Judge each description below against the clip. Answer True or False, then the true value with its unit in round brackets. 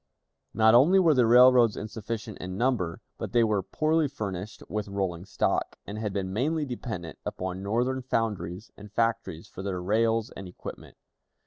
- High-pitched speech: False (110 Hz)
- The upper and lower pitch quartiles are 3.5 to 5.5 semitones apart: True (4.2 semitones)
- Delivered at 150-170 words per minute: True (160 wpm)